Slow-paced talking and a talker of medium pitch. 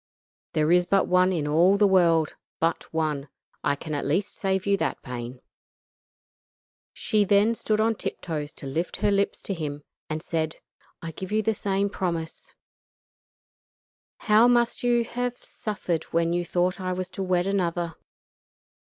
No: average, 165 wpm; medium, 180 Hz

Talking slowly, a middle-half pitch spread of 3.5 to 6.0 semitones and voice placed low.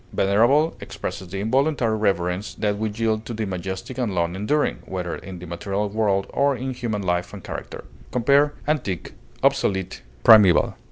No: average, 160 wpm; average, 4.3 semitones; low, 105 Hz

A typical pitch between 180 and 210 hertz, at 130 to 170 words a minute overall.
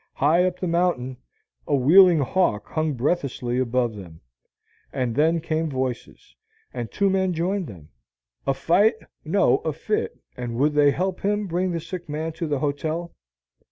No: medium, 155 Hz; average, 160 wpm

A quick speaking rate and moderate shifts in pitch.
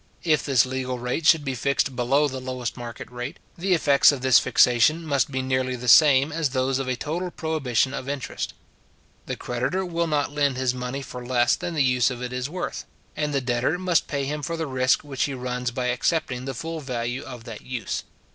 Yes: fast, 215 wpm; average, 3.1 semitones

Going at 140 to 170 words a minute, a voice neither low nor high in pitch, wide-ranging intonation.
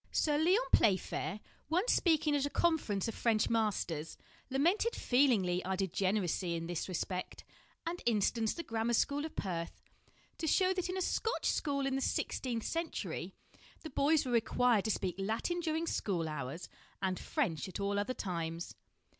No: average, 165 wpm; high, 230 Hz; wide, 8.6 semitones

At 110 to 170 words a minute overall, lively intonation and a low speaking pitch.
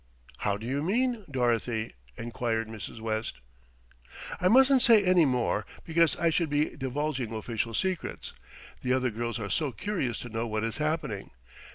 Yes: average, 160 wpm; wide, 6.6 semitones; low, 125 Hz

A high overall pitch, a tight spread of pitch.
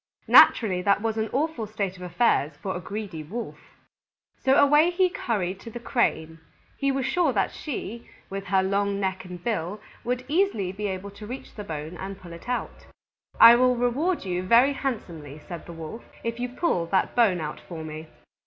No: high, 205 Hz; average, 5.3 semitones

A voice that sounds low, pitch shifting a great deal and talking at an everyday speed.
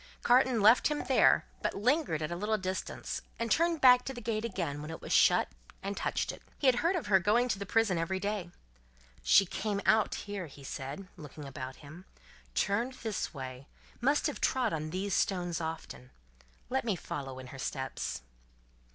No: high, 195 Hz; wide, 7.1 semitones; average, 190 wpm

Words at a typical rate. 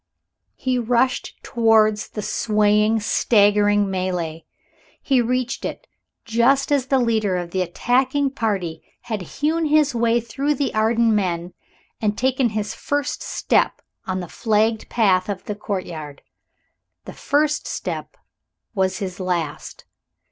No: slow, 130 wpm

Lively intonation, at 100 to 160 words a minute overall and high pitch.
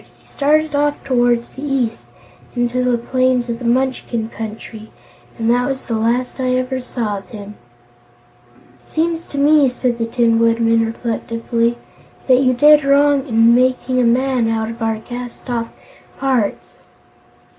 No: narrow, 2.4 semitones; average, 155 wpm; high, 245 Hz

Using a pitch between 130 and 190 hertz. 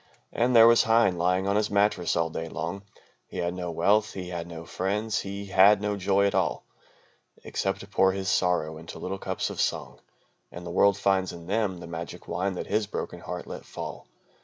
No: very low, 95 Hz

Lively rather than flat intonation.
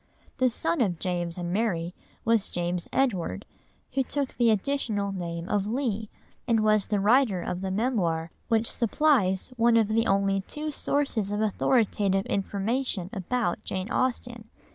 No: average, 4.2 semitones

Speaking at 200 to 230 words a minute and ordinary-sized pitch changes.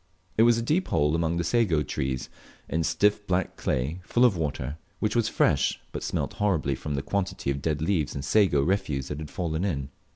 No: fast, 205 wpm; wide, 6.0 semitones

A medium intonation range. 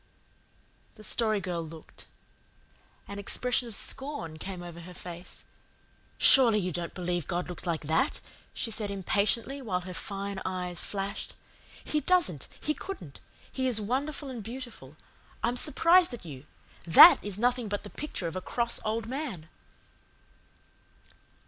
No: wide, 5.8 semitones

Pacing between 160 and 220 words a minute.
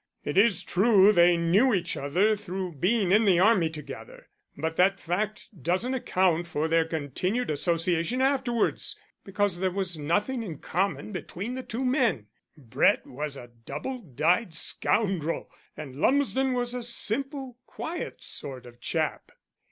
No: average, 145 wpm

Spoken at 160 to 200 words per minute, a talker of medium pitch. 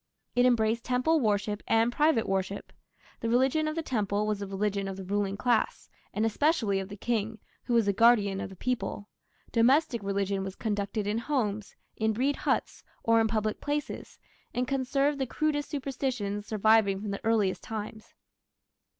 No: average, 170 wpm; high, 220 Hz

